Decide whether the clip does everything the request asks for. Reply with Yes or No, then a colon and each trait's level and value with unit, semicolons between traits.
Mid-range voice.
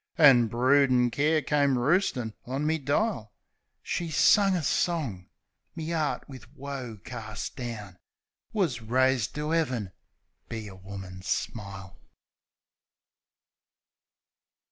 No: low, 130 Hz